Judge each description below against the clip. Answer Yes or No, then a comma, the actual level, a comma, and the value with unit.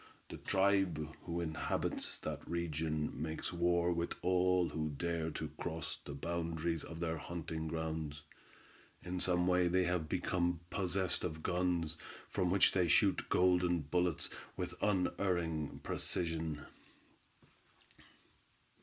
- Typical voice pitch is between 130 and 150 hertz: No, very low, 85 Hz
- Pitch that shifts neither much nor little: No, narrow, 2.1 semitones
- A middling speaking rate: No, slow, 120 wpm